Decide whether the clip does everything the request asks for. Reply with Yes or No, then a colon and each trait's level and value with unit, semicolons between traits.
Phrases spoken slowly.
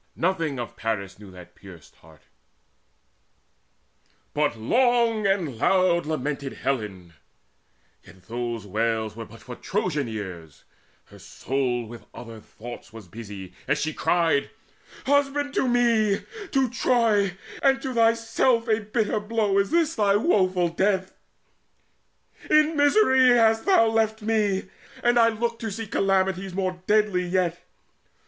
Yes: slow, 130 wpm